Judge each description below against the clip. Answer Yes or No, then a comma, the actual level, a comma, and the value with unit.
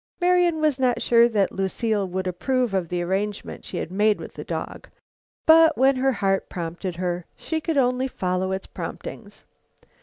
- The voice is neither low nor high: No, high, 210 Hz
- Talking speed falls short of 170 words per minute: No, average, 175 wpm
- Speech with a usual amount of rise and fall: No, wide, 6.1 semitones